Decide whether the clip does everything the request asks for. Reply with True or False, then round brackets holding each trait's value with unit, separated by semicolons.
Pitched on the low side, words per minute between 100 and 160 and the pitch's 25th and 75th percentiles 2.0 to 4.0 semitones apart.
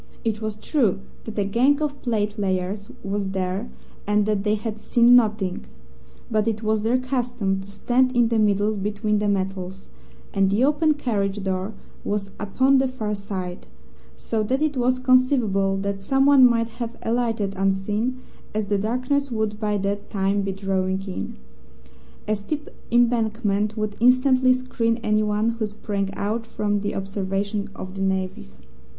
False (210 Hz; 155 wpm; 3.4 semitones)